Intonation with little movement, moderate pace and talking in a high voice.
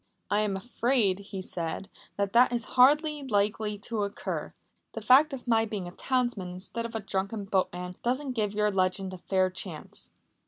No: average, 4.1 semitones; average, 180 wpm; high, 210 Hz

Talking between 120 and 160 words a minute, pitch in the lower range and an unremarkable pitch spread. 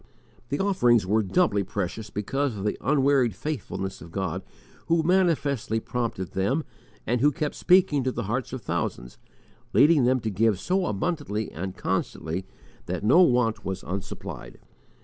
No: average, 150 wpm; low, 120 Hz; wide, 6.9 semitones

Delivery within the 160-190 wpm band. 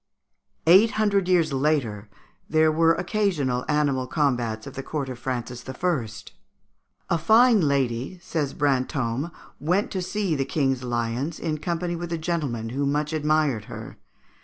No: average, 145 wpm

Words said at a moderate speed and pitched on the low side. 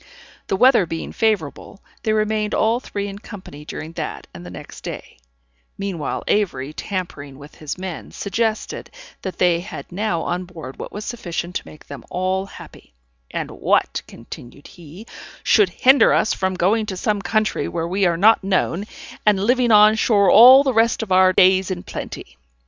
No: average, 175 wpm; high, 190 Hz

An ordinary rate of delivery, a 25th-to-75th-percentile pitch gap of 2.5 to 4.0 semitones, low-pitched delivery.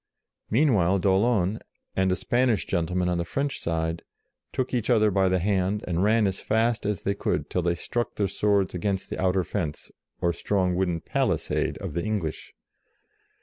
Yes: average, 180 wpm; average, 3.1 semitones; very low, 95 Hz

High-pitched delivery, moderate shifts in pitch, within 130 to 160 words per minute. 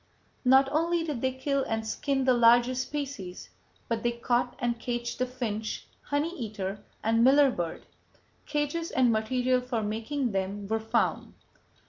Yes: high, 245 Hz; average, 3.4 semitones; average, 150 wpm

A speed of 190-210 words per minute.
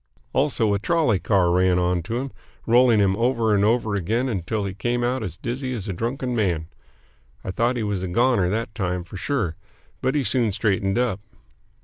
Yes: average, 200 wpm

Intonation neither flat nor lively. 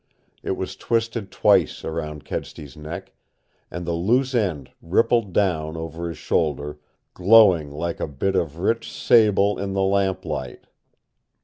Yes: average, 4.6 semitones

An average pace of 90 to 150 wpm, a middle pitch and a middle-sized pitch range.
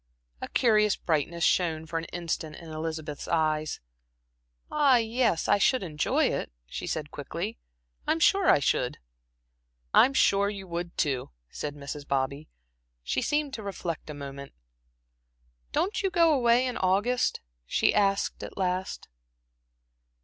No: average, 140 wpm; medium, 175 Hz; wide, 7.4 semitones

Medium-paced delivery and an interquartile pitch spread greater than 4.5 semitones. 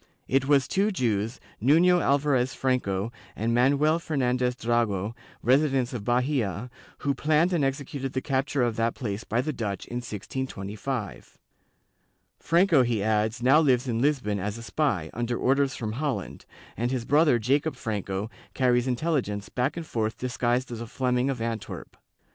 No: average, 155 wpm; average, 3.5 semitones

